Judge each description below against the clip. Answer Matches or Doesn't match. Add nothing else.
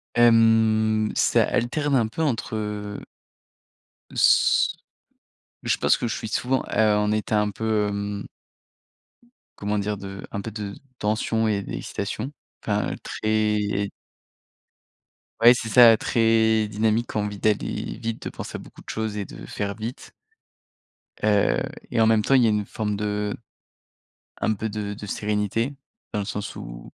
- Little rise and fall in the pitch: Matches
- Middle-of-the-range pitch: Doesn't match